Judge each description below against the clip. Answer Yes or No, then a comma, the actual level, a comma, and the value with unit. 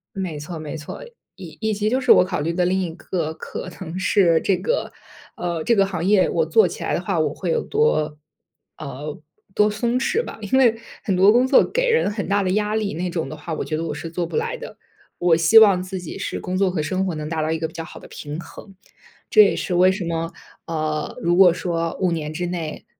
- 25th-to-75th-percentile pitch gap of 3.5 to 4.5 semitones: Yes, average, 4.1 semitones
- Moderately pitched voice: Yes, medium, 180 Hz